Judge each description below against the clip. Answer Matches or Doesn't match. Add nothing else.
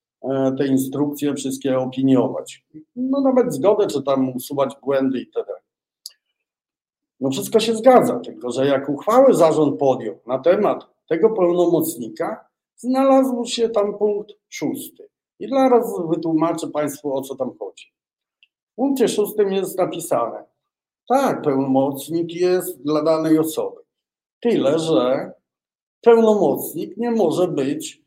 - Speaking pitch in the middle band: Matches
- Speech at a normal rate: Matches